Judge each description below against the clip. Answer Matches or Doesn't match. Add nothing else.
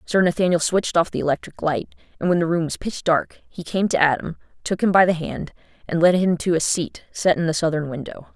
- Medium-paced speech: Doesn't match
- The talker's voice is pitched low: Doesn't match